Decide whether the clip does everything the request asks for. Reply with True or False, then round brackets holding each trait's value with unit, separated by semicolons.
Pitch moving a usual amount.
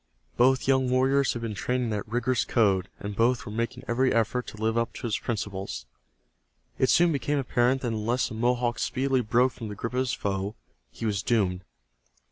True (3.0 semitones)